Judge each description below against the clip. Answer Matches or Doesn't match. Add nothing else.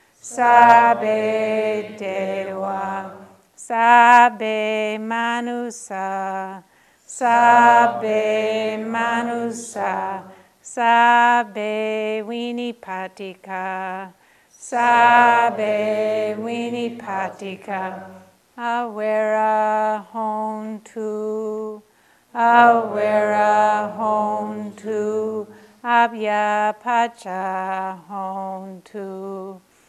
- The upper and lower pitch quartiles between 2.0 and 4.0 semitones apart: Matches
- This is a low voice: Doesn't match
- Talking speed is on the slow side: Matches